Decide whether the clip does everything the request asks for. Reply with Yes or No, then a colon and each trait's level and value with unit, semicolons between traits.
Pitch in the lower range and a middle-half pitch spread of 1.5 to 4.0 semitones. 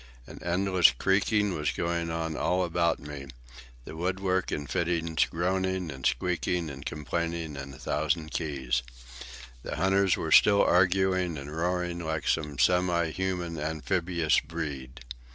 Yes: very low, 85 Hz; average, 3.0 semitones